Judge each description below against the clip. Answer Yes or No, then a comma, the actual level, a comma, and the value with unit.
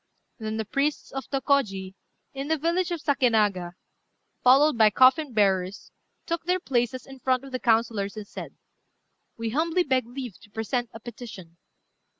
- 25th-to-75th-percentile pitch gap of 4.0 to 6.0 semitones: Yes, average, 4.5 semitones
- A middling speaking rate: Yes, average, 155 wpm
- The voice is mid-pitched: No, very high, 250 Hz